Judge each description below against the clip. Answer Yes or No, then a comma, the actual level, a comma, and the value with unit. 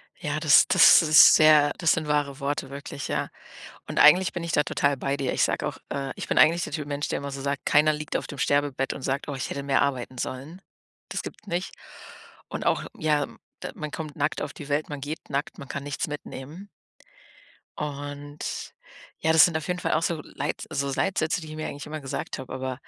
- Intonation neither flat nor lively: No, narrow, 1.9 semitones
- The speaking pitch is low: No, medium, 145 Hz